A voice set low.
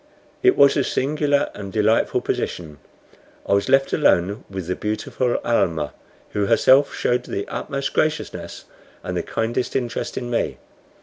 Yes: low, 120 Hz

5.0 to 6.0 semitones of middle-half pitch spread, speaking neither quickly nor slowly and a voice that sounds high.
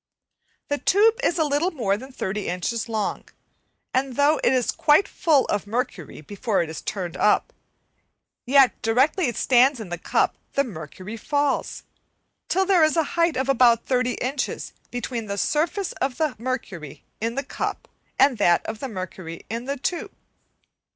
Yes: wide, 5.6 semitones; average, 170 wpm; very high, 250 Hz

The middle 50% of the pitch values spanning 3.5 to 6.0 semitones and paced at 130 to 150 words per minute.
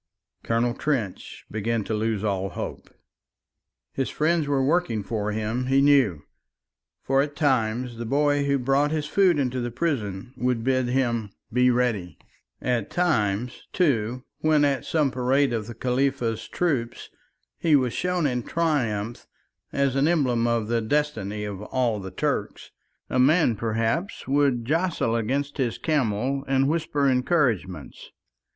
Yes: average, 4.1 semitones; average, 145 wpm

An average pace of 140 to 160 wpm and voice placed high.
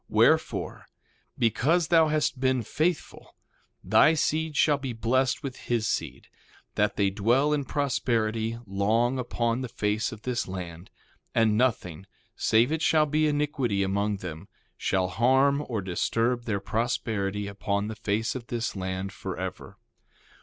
No: average, 145 wpm; low, 115 Hz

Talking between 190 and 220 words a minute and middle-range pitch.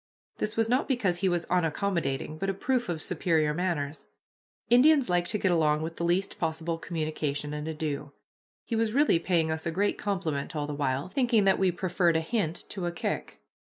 Yes: average, 195 wpm; medium, 170 Hz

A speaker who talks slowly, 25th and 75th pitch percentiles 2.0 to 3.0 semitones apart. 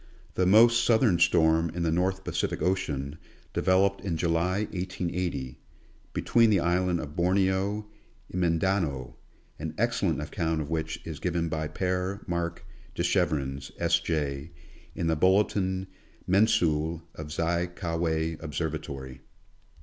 Yes: slow, 125 wpm; average, 2.7 semitones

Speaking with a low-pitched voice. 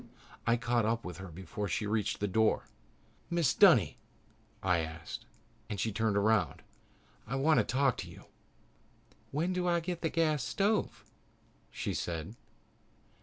Yes: low, 115 Hz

